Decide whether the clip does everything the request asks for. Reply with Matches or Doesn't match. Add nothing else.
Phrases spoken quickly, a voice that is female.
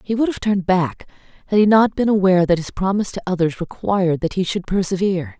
Matches